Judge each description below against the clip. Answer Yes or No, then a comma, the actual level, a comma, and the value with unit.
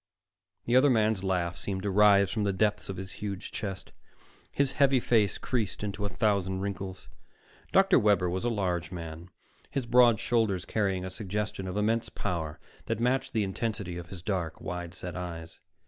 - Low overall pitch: Yes, low, 100 Hz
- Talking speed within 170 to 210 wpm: Yes, average, 180 wpm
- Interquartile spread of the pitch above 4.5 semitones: No, average, 3.1 semitones